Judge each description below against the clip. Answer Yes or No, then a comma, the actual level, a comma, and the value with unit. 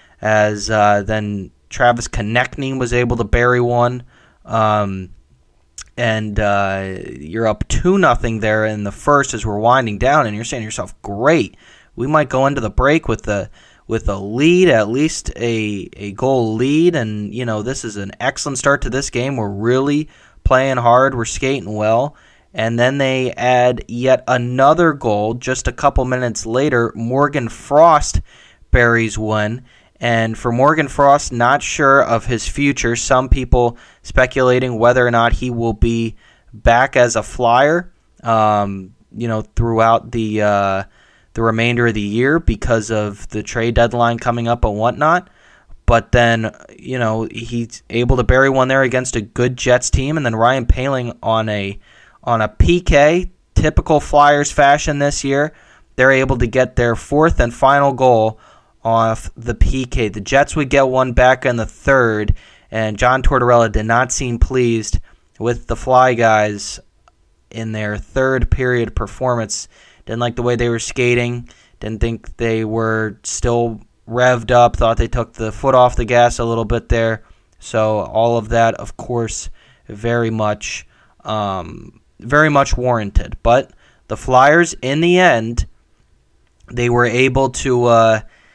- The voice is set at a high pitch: No, low, 120 Hz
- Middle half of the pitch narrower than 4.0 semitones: Yes, average, 3.0 semitones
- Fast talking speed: No, average, 160 wpm